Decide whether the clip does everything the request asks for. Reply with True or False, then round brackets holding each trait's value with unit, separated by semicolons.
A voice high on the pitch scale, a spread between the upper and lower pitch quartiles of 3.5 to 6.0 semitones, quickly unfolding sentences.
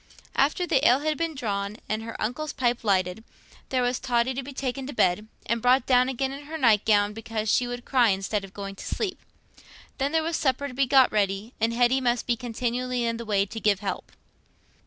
True (245 Hz; 3.8 semitones; 220 wpm)